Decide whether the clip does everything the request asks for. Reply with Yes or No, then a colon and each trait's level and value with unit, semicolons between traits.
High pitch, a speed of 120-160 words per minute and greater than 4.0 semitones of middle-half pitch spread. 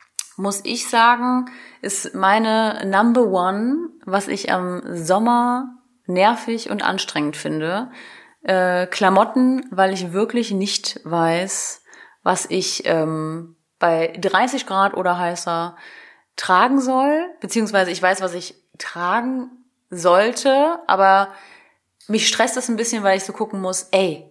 Yes: high, 195 Hz; slow, 125 wpm; average, 4.7 semitones